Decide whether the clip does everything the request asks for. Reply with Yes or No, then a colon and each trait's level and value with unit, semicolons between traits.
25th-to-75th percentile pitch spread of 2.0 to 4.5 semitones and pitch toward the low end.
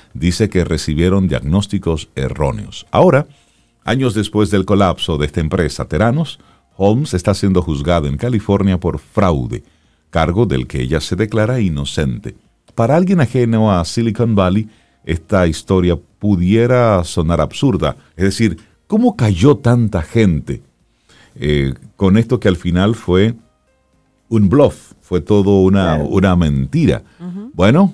No: average, 5.0 semitones; low, 100 Hz